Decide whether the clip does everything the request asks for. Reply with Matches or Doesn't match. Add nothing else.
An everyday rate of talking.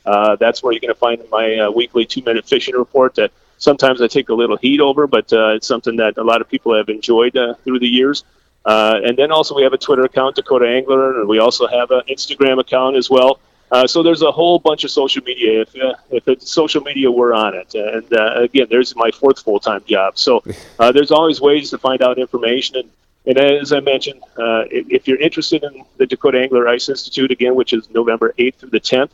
Doesn't match